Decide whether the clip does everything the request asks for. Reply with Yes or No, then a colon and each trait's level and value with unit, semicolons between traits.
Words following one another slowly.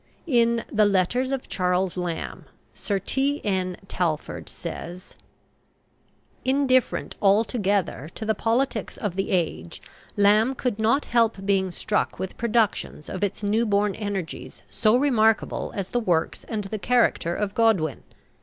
Yes: slow, 130 wpm